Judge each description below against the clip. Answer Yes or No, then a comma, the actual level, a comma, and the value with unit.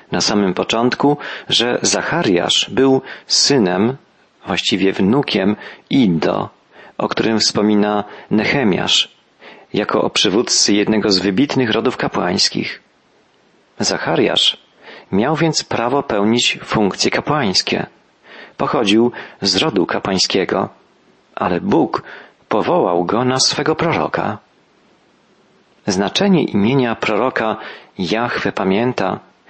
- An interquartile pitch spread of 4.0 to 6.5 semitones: Yes, average, 4.6 semitones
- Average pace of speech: No, slow, 90 wpm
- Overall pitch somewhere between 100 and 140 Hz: Yes, low, 110 Hz